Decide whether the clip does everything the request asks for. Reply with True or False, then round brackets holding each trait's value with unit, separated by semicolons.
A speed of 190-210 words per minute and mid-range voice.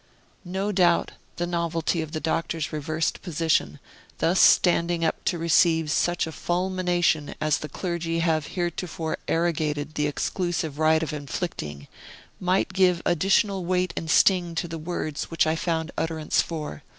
False (150 wpm; 165 Hz)